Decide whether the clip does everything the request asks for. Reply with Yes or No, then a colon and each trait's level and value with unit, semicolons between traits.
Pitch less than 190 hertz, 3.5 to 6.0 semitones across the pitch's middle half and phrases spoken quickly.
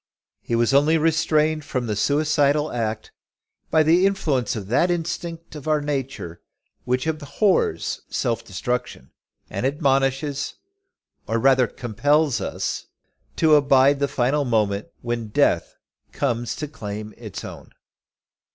No: medium, 140 Hz; average, 4.5 semitones; slow, 135 wpm